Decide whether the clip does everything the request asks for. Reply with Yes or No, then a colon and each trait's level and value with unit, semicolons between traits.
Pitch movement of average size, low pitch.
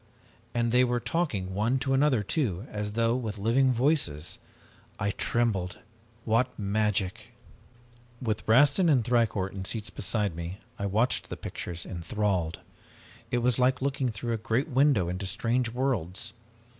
Yes: average, 4.3 semitones; low, 115 Hz